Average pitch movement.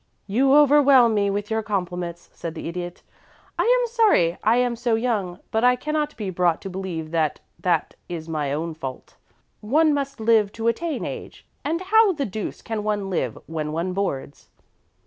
No: wide, 7.3 semitones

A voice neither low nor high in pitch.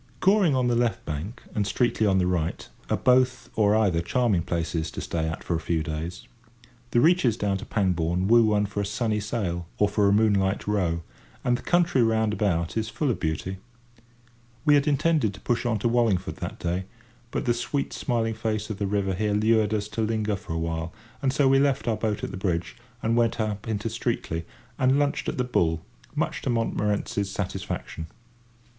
No: low, 105 Hz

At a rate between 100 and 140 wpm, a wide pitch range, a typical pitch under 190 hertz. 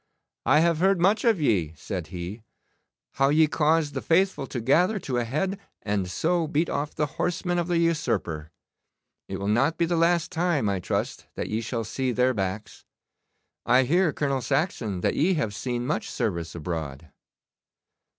No: average, 175 wpm; wide, 8.1 semitones; low, 135 Hz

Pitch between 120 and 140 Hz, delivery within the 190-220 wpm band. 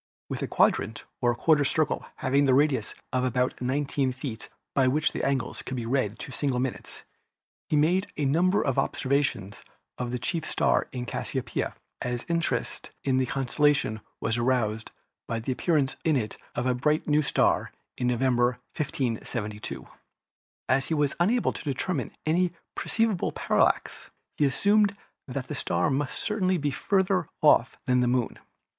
No: low, 135 Hz; average, 165 wpm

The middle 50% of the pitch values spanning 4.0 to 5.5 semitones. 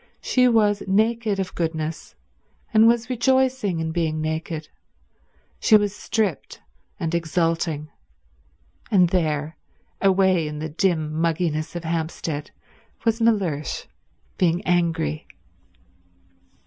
Yes: average, 4.7 semitones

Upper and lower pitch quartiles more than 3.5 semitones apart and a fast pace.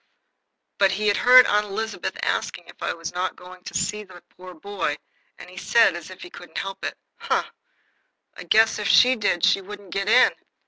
No: narrow, 2.6 semitones; fast, 210 wpm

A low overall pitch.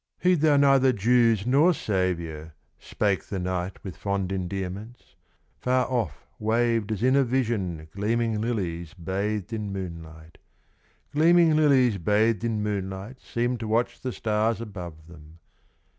Yes: low, 105 Hz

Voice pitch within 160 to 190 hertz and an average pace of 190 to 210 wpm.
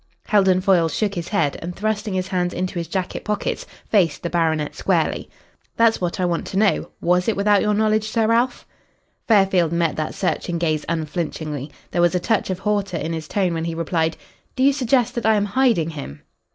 Yes: medium, 185 Hz; fast, 205 wpm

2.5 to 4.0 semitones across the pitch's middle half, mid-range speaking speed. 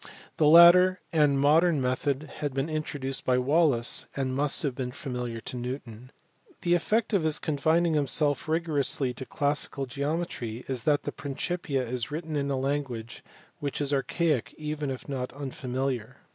Yes: average, 3.1 semitones; average, 160 wpm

